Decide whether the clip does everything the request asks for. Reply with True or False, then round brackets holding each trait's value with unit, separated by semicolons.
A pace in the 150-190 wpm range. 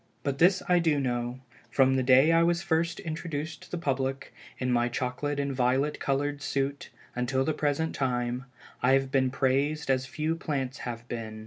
True (185 wpm)